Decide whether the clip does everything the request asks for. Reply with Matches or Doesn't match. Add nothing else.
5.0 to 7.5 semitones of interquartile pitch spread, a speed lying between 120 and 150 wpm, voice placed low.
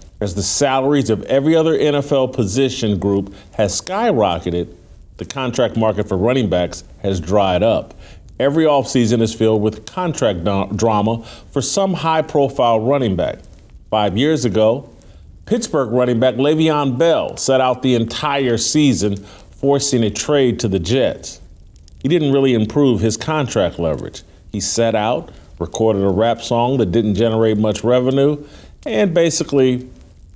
Matches